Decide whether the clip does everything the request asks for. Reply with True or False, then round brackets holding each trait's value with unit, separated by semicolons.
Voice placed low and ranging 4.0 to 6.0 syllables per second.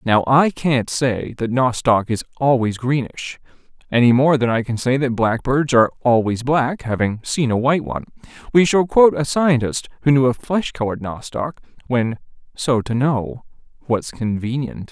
True (125 Hz; 4.8 syllables/s)